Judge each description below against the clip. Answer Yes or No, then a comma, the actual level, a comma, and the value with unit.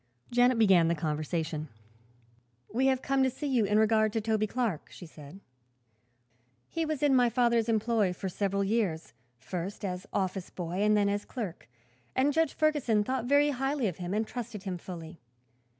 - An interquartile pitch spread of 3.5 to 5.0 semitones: No, wide, 5.4 semitones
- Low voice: No, high, 215 Hz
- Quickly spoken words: No, average, 175 wpm